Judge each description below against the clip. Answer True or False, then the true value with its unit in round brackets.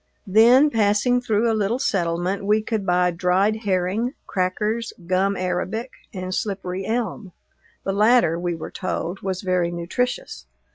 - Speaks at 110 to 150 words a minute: True (140 wpm)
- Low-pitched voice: False (195 Hz)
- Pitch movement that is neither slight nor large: True (3.5 semitones)